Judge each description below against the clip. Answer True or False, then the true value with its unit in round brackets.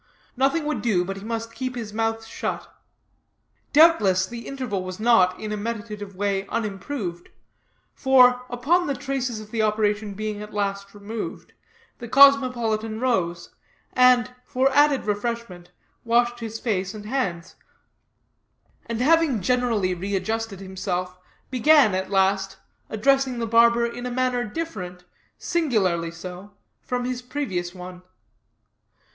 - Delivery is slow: True (130 wpm)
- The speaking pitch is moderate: False (225 Hz)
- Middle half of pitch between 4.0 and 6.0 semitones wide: True (4.3 semitones)